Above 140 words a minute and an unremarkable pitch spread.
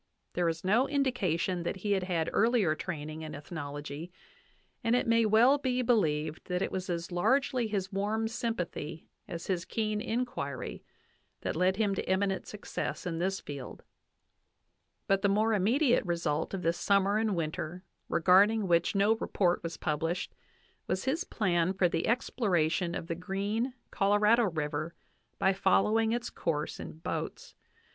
Yes: average, 155 wpm; average, 4.7 semitones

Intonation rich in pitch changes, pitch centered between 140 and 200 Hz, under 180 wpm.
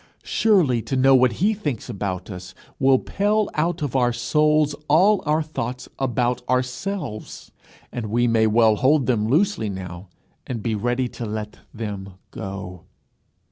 No: wide, 5.9 semitones; low, 125 Hz; average, 150 wpm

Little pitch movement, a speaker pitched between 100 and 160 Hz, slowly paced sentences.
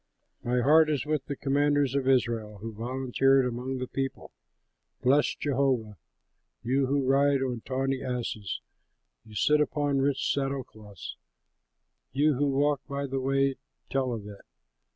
No: narrow, 2.2 semitones; low, 135 Hz; average, 145 wpm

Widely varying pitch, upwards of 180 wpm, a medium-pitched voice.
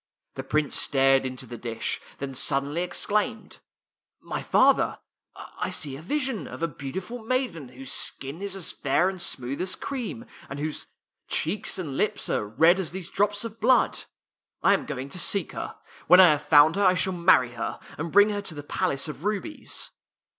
Yes: wide, 6.6 semitones; average, 195 wpm; medium, 170 Hz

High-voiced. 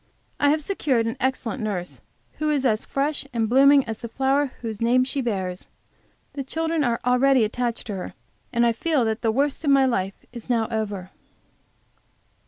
Yes: high, 245 Hz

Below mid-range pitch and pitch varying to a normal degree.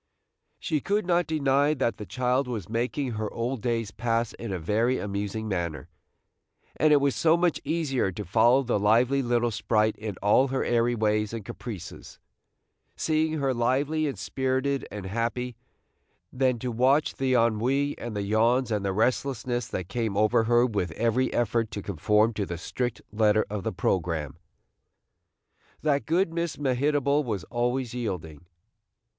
Yes: low, 120 Hz; average, 4.1 semitones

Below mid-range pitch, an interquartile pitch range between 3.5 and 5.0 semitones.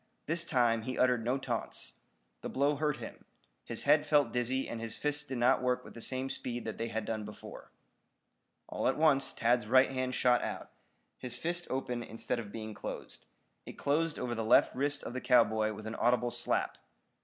No: low, 125 Hz; average, 2.9 semitones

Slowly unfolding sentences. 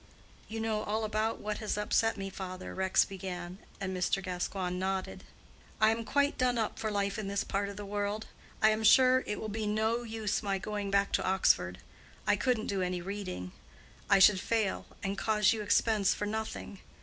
No: average, 195 wpm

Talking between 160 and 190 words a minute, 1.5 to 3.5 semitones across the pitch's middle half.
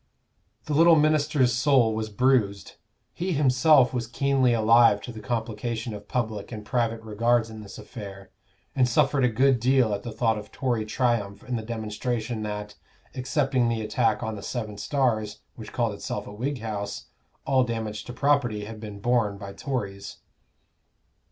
Yes: average, 165 wpm; average, 3.2 semitones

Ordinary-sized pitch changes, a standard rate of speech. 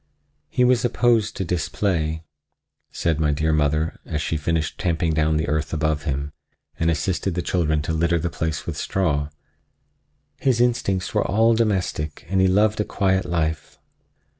Yes: average, 3.8 semitones; average, 165 wpm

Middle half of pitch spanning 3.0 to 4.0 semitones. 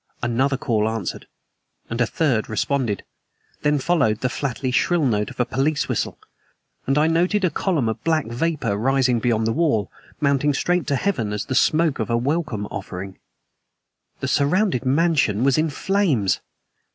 No: wide, 5.6 semitones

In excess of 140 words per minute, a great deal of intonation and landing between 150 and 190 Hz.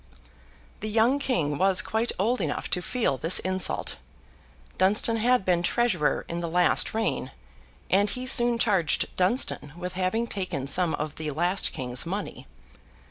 No: average, 150 wpm; average, 5.0 semitones; medium, 185 Hz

